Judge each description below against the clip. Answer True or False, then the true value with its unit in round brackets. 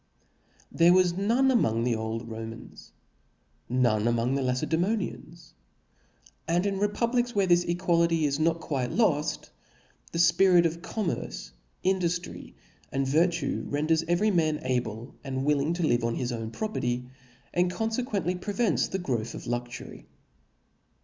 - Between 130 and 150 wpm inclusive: True (140 wpm)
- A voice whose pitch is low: False (165 Hz)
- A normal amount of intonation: False (6.6 semitones)